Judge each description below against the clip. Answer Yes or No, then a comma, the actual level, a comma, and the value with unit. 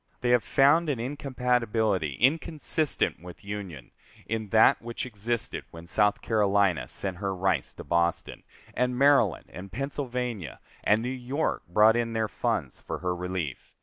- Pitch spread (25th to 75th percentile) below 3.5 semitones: No, average, 4.8 semitones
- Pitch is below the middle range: Yes, low, 110 Hz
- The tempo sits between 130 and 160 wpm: Yes, average, 150 wpm